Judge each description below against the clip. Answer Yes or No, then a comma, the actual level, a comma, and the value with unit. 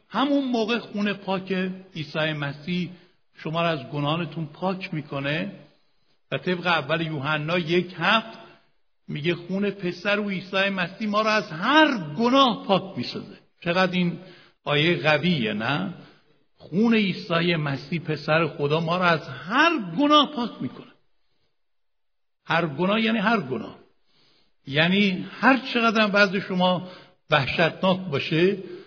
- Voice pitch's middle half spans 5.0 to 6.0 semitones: No, average, 4.1 semitones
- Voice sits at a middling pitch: Yes, medium, 180 Hz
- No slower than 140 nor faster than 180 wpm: No, average, 125 wpm